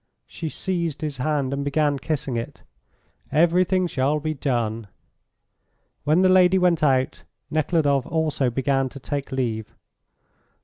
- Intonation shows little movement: No, average, 3.4 semitones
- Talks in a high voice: No, medium, 145 Hz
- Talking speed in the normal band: No, slow, 130 wpm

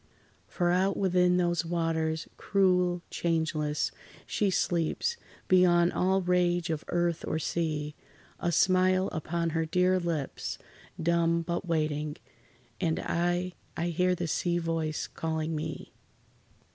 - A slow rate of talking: Yes, slow, 120 wpm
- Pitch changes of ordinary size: No, narrow, 1.9 semitones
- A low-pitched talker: No, medium, 170 Hz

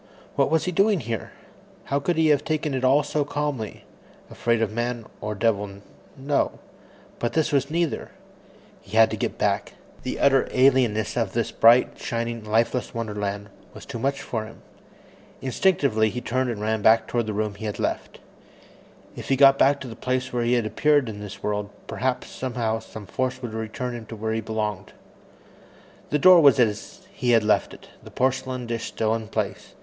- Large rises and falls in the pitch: No, average, 3.7 semitones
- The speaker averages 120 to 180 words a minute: No, average, 190 wpm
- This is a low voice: Yes, low, 120 Hz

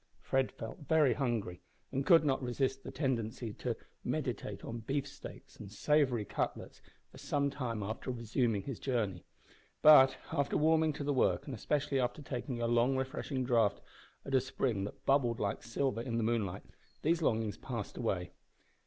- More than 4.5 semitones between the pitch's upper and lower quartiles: No, average, 3.5 semitones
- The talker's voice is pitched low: Yes, low, 125 Hz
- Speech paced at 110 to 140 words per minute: No, average, 165 wpm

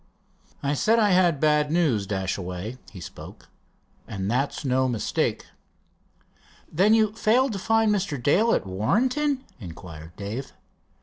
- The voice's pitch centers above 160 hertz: No, medium, 145 Hz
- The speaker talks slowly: Yes, slow, 130 wpm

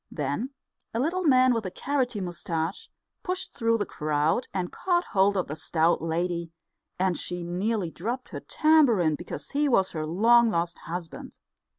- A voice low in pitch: No, high, 190 Hz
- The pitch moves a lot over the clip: Yes, wide, 6.4 semitones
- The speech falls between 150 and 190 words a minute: Yes, average, 165 wpm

